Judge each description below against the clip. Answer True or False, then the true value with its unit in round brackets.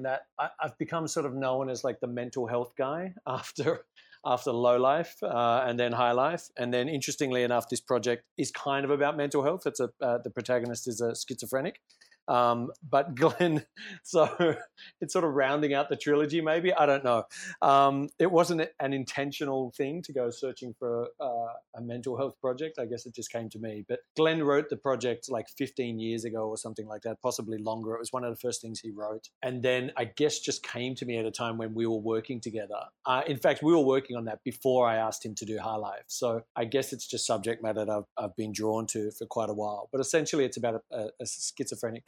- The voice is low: True (125 Hz)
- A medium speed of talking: False (225 wpm)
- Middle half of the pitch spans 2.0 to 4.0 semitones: True (3.7 semitones)